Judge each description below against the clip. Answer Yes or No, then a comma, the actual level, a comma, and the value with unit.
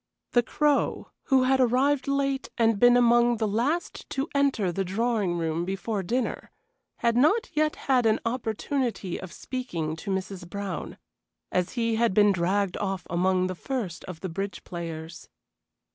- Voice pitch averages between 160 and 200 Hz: No, high, 220 Hz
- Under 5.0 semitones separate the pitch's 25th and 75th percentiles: No, wide, 5.5 semitones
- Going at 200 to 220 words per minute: No, average, 160 wpm